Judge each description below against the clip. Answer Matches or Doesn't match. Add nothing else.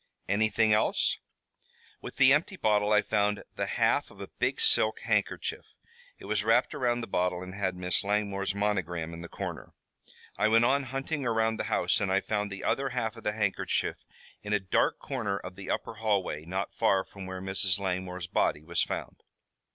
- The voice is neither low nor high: Doesn't match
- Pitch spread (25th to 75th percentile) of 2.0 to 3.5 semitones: Matches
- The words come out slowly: Doesn't match